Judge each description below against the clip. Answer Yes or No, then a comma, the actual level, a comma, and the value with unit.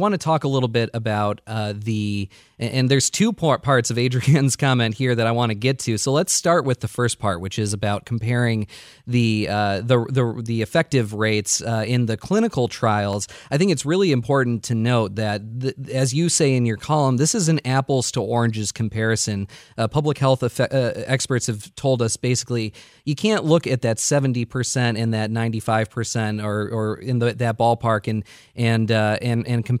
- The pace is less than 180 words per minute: No, average, 200 wpm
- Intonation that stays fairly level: No, average, 3.3 semitones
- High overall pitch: No, low, 120 Hz